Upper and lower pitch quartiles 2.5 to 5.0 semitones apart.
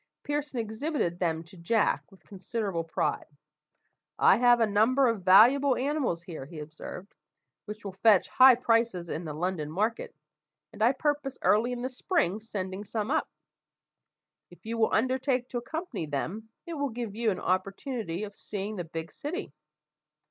No: wide, 5.4 semitones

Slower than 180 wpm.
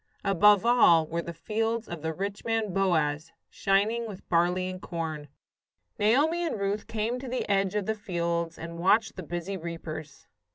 Yes: average, 170 wpm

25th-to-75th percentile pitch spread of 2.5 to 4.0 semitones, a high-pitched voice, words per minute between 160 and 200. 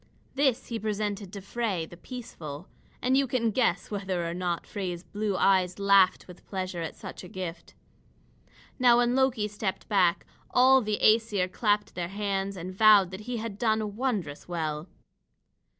Yes: average, 3.7 semitones; high, 200 Hz; average, 165 wpm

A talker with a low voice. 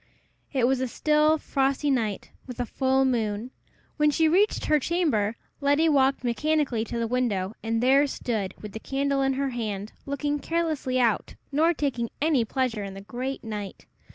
No: very high, 260 Hz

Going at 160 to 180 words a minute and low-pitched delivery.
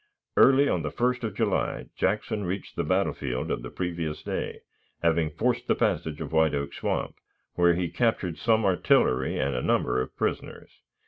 Yes: average, 175 wpm; very low, 85 Hz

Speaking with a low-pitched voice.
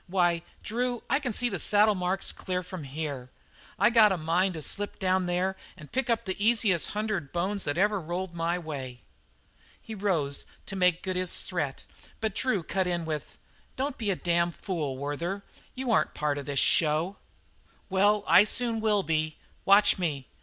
No: medium, 185 Hz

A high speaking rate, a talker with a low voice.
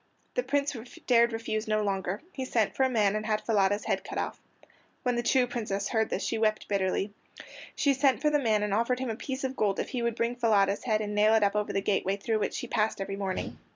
No: fast, 250 wpm; high, 220 Hz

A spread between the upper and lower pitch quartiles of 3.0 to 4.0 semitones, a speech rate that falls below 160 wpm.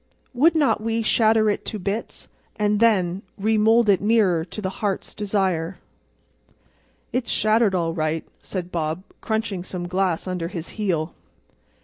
Yes: average, 3.7 semitones; slow, 135 wpm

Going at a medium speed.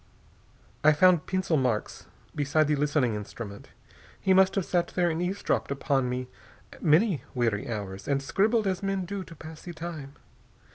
Yes: average, 160 wpm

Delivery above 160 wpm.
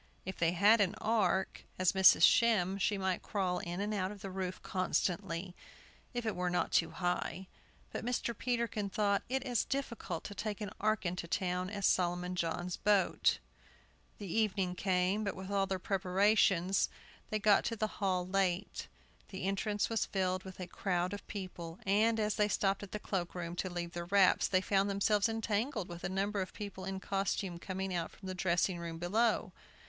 Yes: average, 185 wpm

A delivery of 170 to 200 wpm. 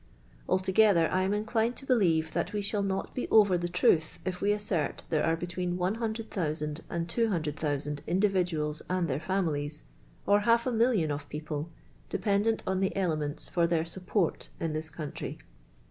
Yes: average, 175 wpm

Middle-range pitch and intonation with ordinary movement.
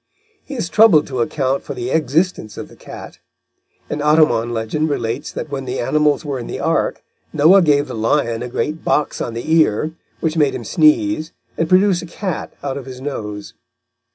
Yes: medium, 145 Hz; average, 4.6 semitones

